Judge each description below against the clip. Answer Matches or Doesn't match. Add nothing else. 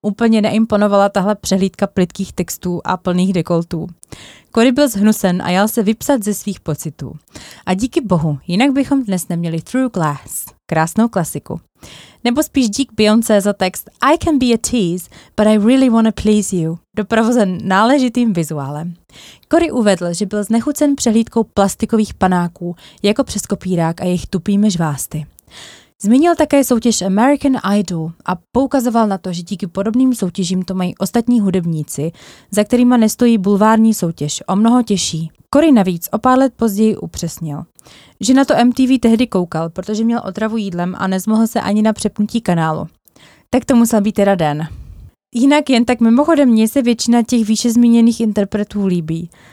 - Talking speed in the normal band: Matches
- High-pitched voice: Matches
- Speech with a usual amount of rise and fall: Matches